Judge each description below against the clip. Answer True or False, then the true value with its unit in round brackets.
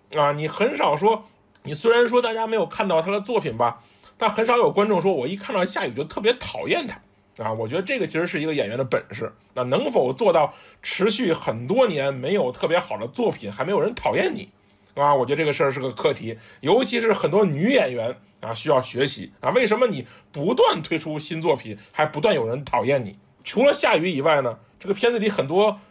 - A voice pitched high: True (195 Hz)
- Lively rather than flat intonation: True (7.5 semitones)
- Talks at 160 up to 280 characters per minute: False (325 characters per minute)